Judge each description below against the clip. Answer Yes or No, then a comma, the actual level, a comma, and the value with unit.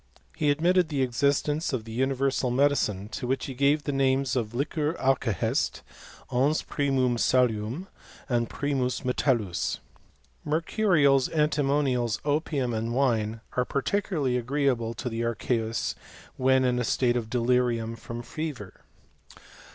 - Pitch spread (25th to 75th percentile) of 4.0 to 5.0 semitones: No, average, 3.4 semitones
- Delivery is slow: Yes, slow, 125 wpm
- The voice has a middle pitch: No, low, 130 Hz